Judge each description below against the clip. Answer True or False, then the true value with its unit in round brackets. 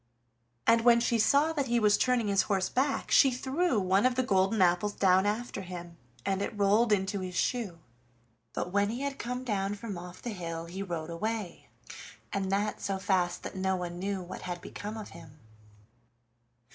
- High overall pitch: True (200 Hz)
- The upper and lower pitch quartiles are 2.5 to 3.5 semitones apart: False (4.0 semitones)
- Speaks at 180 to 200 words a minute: True (190 wpm)